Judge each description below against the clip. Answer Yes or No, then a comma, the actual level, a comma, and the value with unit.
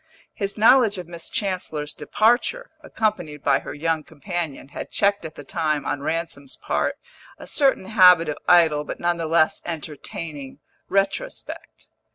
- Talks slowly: No, average, 150 wpm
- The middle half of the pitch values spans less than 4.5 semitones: No, average, 4.8 semitones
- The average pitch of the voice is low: No, medium, 170 Hz